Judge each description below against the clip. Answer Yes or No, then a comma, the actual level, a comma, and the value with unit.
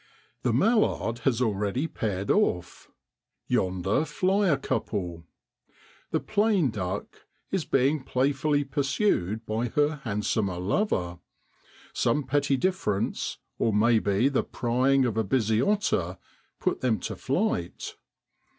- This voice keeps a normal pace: No, slow, 115 wpm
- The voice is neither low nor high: No, low, 120 Hz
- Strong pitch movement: Yes, wide, 6.1 semitones